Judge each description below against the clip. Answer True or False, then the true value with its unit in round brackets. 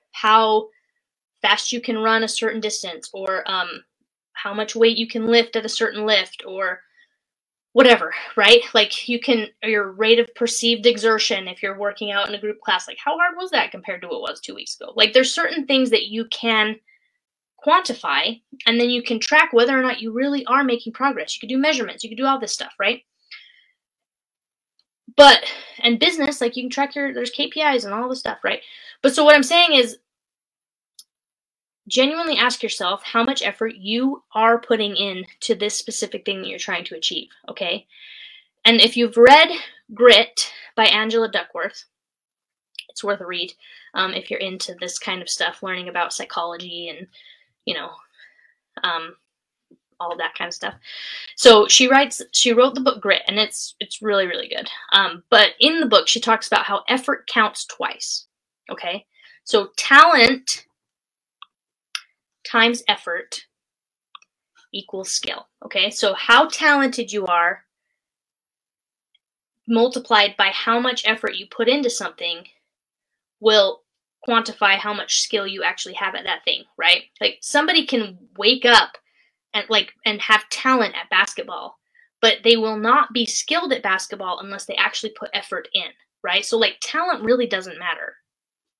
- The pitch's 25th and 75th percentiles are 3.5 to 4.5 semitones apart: True (4.2 semitones)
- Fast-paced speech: False (170 wpm)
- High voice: True (230 Hz)